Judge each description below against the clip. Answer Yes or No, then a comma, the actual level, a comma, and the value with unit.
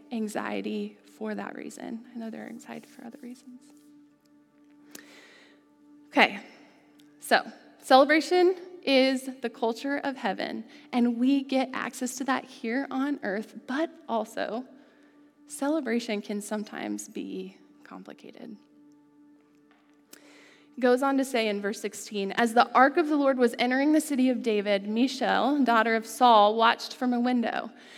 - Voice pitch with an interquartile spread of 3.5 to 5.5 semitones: Yes, average, 4.7 semitones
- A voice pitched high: Yes, very high, 250 Hz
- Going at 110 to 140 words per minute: Yes, slow, 135 wpm